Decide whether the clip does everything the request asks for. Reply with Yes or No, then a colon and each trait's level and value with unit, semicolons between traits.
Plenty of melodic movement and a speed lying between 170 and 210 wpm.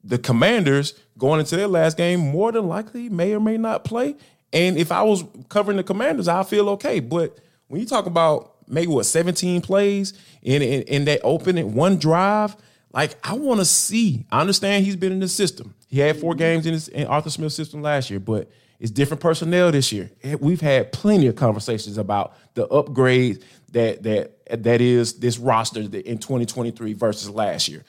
Yes: wide, 7.0 semitones; average, 200 wpm